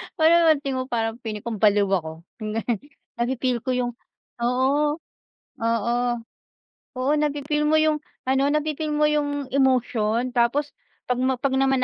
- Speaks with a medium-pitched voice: No, very high, 260 Hz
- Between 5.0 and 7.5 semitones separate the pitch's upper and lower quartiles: No, average, 3.8 semitones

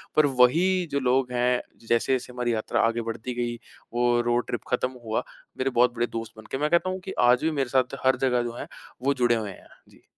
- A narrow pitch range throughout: Yes, narrow, 1.9 semitones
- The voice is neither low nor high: No, low, 125 Hz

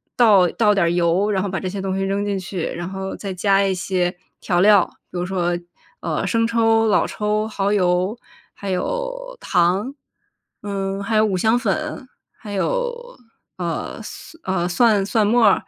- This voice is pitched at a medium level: No, high, 200 Hz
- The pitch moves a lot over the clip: No, average, 3.1 semitones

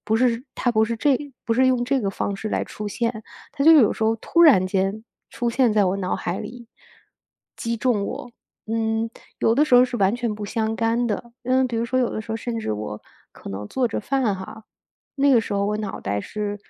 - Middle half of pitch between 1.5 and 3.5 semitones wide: Yes, average, 2.8 semitones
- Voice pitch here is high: Yes, high, 225 Hz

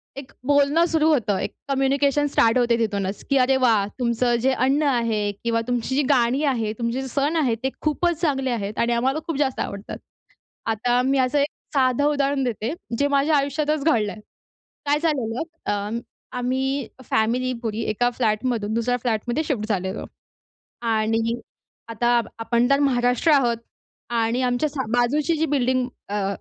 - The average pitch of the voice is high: Yes, very high, 250 Hz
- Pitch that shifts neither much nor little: Yes, average, 3.5 semitones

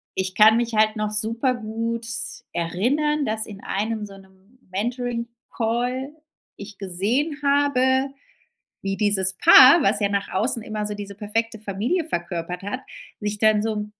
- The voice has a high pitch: Yes, high, 220 Hz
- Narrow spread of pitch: No, average, 3.3 semitones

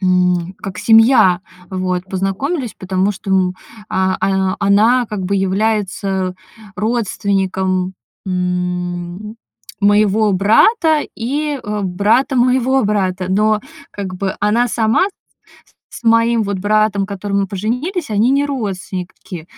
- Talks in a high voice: Yes, high, 200 Hz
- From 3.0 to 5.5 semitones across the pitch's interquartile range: Yes, average, 3.3 semitones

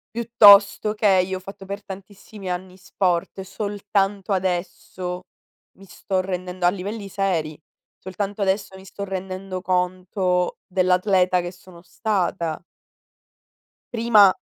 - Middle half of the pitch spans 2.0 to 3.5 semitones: No, narrow, 1.6 semitones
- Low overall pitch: No, high, 190 Hz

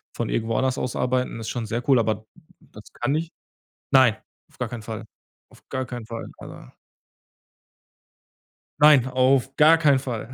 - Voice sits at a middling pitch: No, low, 125 Hz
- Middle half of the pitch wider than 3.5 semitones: No, average, 2.8 semitones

